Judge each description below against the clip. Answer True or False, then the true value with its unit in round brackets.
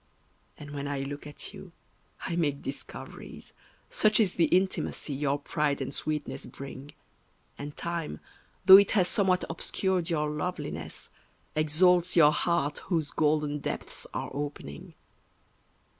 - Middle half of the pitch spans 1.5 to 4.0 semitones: True (3.5 semitones)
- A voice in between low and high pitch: True (150 Hz)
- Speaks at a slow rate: True (130 wpm)